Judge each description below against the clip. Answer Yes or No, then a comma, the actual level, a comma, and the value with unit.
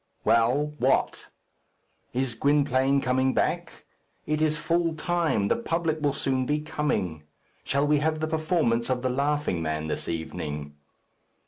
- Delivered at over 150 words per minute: No, average, 140 wpm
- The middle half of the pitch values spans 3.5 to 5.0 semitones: Yes, average, 4.6 semitones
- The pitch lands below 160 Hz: Yes, medium, 140 Hz